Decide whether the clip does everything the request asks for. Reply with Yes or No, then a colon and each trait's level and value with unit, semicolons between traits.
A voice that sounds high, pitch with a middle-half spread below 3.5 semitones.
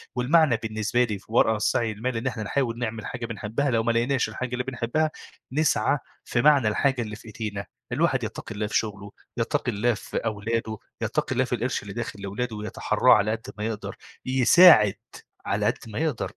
No: low, 115 Hz; average, 3.0 semitones